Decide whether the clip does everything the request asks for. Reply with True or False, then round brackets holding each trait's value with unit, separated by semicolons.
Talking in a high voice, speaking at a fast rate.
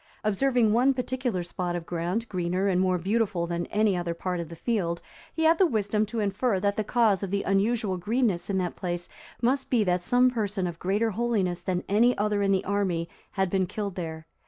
True (200 Hz; 210 wpm)